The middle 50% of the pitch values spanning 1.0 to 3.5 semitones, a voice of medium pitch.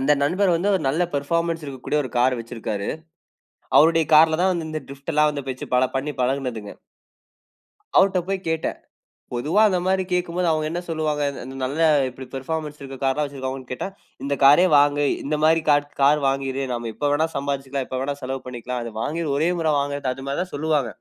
Yes: average, 3.2 semitones; medium, 145 Hz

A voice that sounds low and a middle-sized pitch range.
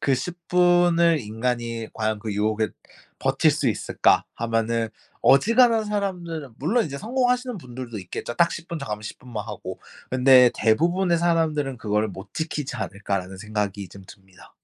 No: low, 130 Hz; wide, 7.9 semitones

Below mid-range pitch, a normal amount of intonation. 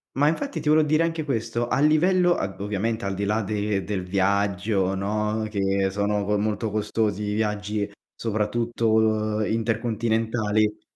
No: low, 105 Hz; narrow, 2.1 semitones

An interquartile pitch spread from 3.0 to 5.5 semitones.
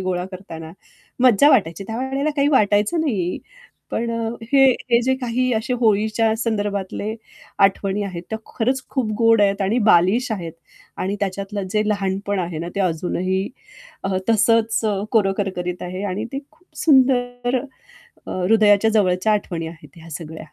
Yes: average, 3.9 semitones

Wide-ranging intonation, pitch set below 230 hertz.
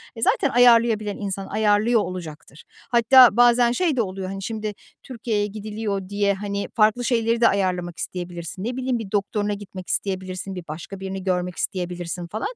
No: average, 3.6 semitones; high, 205 Hz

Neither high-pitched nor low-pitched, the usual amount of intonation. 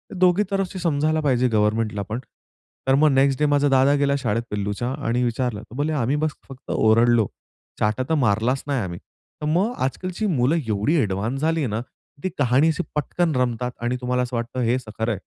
No: low, 130 Hz; average, 4.6 semitones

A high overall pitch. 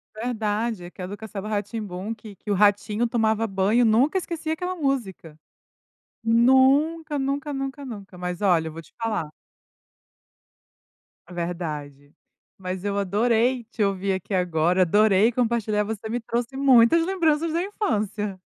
Yes: high, 220 Hz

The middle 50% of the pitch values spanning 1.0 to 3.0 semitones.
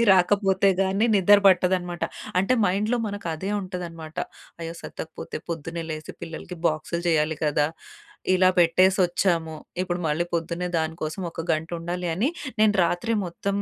Yes: narrow, 2.6 semitones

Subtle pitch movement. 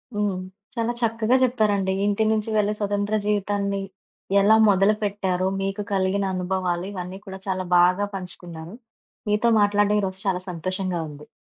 Yes: narrow, 2.0 semitones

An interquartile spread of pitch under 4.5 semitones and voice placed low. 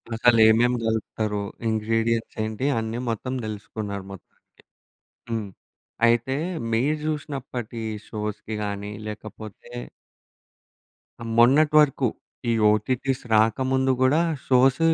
Yes: average, 3.3 semitones; low, 115 Hz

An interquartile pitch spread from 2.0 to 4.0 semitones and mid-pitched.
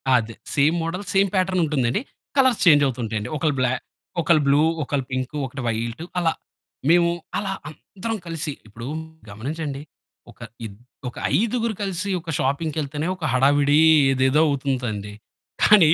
No: average, 4.8 semitones; medium, 145 Hz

